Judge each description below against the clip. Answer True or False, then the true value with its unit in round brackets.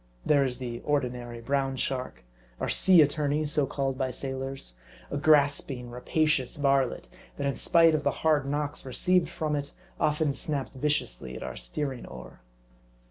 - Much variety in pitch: False (2.8 semitones)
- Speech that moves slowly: False (160 wpm)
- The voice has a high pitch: False (140 Hz)